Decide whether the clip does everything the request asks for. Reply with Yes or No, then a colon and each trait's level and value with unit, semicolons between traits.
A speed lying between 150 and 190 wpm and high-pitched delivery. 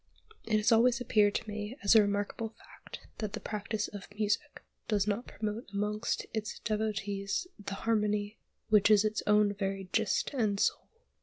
Yes: average, 165 wpm; high, 210 Hz